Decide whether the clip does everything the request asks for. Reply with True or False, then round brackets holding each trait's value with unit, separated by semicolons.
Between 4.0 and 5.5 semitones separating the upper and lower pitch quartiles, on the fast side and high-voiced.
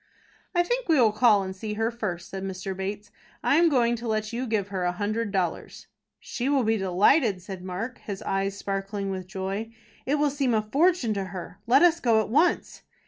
True (4.4 semitones; 210 wpm; 215 Hz)